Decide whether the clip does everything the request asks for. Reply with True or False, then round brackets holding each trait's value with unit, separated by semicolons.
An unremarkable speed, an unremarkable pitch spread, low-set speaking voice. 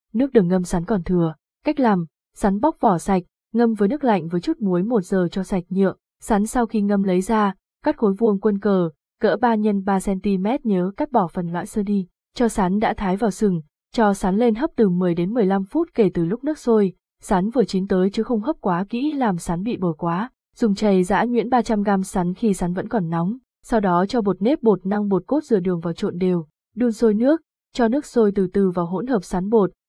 False (240 wpm; 3.8 semitones; 205 Hz)